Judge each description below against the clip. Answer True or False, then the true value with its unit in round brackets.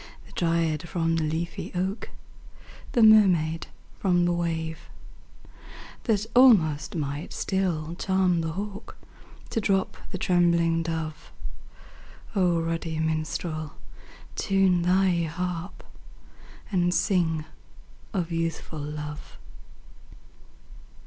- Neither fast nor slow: False (95 wpm)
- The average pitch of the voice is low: False (170 Hz)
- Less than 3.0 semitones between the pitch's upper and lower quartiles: True (2.6 semitones)